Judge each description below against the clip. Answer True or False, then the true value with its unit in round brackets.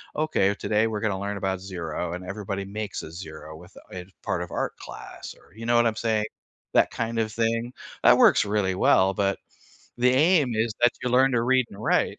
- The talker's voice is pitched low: True (105 Hz)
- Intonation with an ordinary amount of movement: True (3.6 semitones)